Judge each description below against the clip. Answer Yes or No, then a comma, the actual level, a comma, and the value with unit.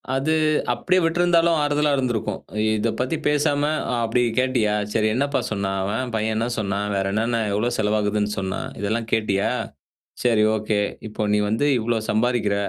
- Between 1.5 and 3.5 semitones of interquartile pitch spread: No, average, 3.9 semitones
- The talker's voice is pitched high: No, low, 110 Hz